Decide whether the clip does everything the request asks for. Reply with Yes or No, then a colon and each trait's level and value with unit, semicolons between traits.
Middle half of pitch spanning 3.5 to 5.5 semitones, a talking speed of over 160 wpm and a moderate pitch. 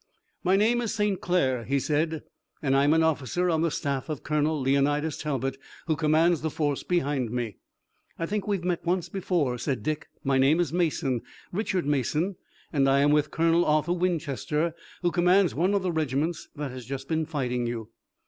Yes: average, 4.1 semitones; average, 185 wpm; medium, 155 Hz